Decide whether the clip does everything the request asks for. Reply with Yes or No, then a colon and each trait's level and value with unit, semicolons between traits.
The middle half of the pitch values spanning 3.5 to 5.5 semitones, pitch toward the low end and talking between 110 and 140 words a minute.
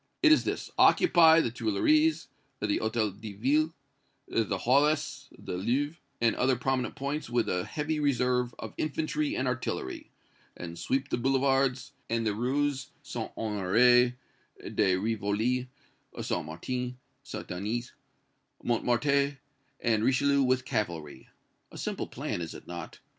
Yes: average, 4.3 semitones; low, 125 Hz; slow, 135 wpm